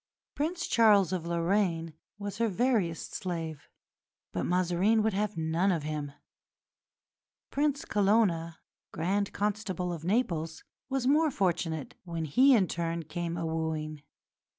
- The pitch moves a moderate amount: Yes, average, 4.4 semitones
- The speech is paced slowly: Yes, slow, 130 wpm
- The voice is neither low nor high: Yes, medium, 180 Hz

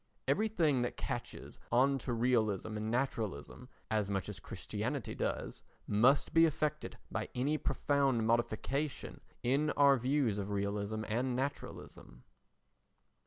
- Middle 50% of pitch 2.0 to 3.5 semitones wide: No, average, 4.4 semitones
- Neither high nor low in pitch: No, low, 125 Hz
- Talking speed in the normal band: No, slow, 120 wpm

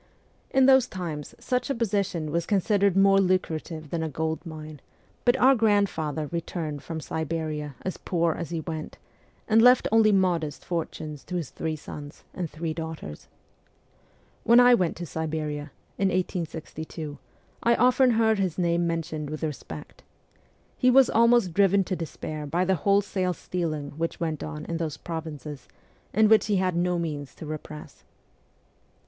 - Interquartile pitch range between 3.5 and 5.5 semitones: Yes, average, 4.2 semitones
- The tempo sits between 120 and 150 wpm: No, average, 165 wpm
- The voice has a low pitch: No, medium, 170 Hz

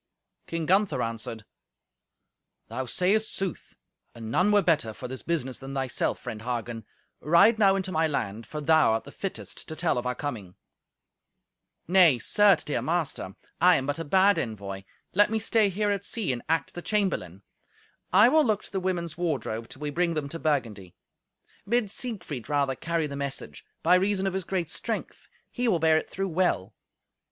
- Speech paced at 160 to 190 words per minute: Yes, average, 180 wpm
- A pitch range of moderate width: No, wide, 7.2 semitones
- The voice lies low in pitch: No, medium, 160 Hz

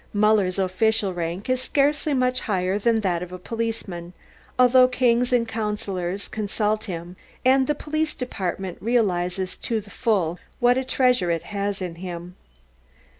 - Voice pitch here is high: Yes, high, 210 Hz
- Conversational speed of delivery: Yes, average, 150 wpm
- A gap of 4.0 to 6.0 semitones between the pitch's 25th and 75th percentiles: Yes, average, 5.3 semitones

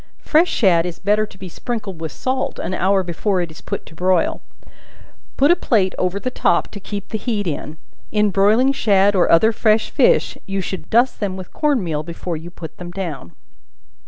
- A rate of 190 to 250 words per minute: Yes, average, 200 wpm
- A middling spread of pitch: Yes, average, 4.0 semitones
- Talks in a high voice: Yes, high, 195 Hz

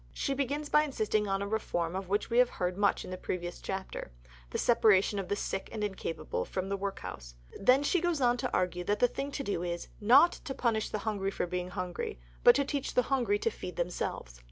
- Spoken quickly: Yes, fast, 225 wpm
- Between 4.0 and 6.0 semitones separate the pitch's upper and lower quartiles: Yes, average, 5.3 semitones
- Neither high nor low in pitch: No, high, 205 Hz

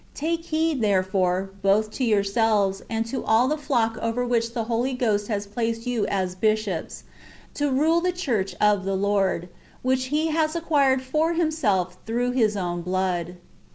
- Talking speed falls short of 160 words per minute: No, average, 170 wpm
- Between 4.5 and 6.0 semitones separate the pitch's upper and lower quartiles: Yes, average, 5.2 semitones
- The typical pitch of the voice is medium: No, high, 225 Hz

